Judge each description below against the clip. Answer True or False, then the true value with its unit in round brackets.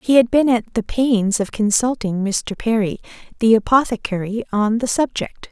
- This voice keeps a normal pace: True (165 wpm)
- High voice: True (225 Hz)